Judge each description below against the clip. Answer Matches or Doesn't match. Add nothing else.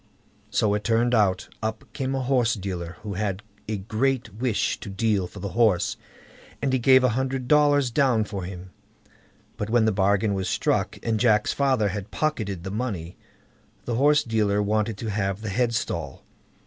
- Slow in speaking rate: Doesn't match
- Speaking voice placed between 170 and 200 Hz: Doesn't match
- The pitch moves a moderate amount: Matches